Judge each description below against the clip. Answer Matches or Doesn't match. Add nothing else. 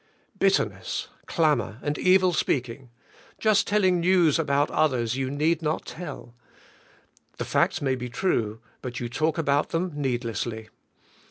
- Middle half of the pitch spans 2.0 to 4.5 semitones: Doesn't match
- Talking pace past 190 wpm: Doesn't match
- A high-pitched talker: Doesn't match